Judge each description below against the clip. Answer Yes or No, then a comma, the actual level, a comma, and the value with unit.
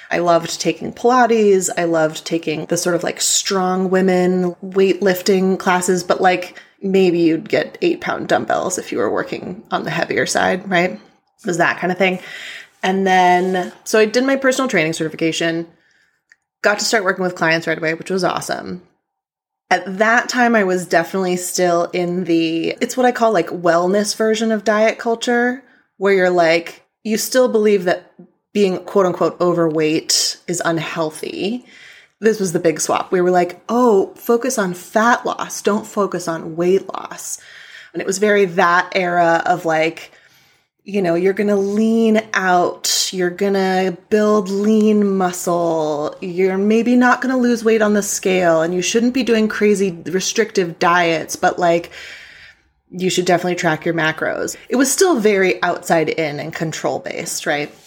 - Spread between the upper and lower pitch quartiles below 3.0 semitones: No, average, 3.7 semitones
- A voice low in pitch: No, medium, 185 Hz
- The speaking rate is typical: Yes, average, 170 wpm